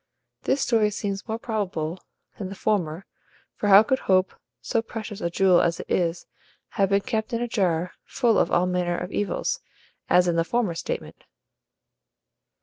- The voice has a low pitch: No, high, 195 Hz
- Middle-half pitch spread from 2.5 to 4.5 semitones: Yes, average, 3.7 semitones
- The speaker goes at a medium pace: Yes, average, 170 wpm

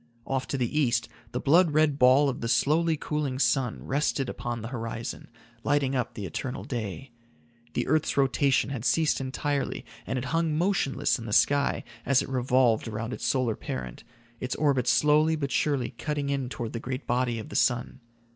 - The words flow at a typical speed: Yes, average, 185 wpm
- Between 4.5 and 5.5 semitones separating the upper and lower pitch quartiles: No, average, 3.2 semitones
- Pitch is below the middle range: Yes, low, 130 Hz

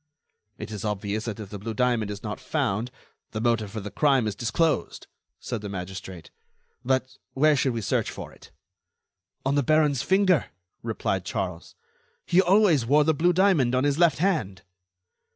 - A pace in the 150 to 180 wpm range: Yes, average, 170 wpm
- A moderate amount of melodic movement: No, wide, 6.6 semitones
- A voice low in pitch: Yes, low, 125 Hz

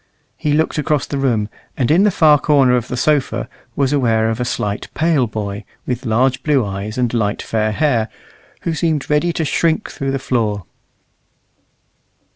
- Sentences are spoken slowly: No, average, 175 wpm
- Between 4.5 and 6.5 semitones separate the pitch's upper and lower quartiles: Yes, average, 5.1 semitones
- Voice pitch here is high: No, low, 130 Hz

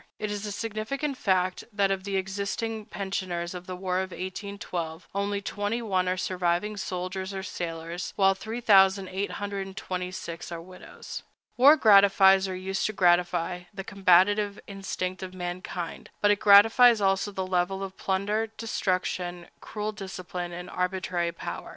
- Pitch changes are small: Yes, narrow, 1.9 semitones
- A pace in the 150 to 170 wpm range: No, average, 140 wpm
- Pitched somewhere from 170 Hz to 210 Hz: Yes, high, 190 Hz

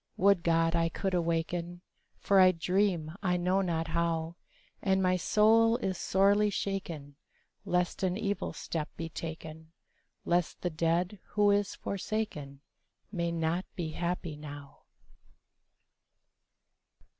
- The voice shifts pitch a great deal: No, average, 2.9 semitones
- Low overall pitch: No, medium, 175 Hz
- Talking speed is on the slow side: Yes, slow, 125 wpm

